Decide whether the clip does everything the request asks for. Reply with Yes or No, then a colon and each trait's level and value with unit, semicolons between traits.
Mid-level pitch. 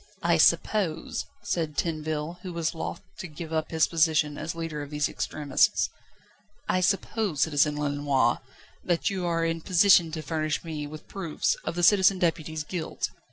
Yes: medium, 160 Hz